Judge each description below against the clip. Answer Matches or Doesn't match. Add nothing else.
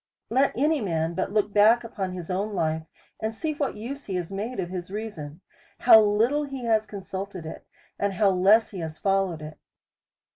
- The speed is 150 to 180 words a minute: Doesn't match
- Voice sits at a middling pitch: Doesn't match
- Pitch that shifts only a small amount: Doesn't match